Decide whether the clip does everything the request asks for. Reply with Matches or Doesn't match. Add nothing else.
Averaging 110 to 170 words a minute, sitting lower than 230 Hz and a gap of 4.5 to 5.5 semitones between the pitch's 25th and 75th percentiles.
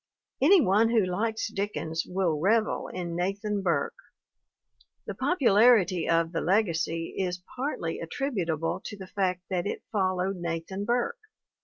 Doesn't match